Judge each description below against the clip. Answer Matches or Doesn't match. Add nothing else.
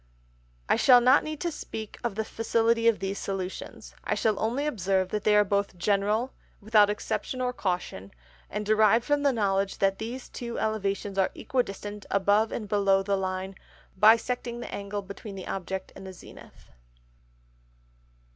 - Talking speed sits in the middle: Matches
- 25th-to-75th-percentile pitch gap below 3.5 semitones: Matches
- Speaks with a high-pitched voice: Matches